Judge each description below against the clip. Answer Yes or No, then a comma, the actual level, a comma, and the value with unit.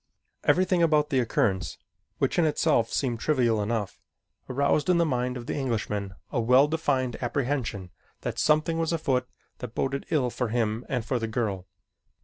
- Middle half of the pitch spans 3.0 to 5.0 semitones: Yes, average, 4.7 semitones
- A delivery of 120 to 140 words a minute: No, average, 165 wpm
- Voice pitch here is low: Yes, low, 125 Hz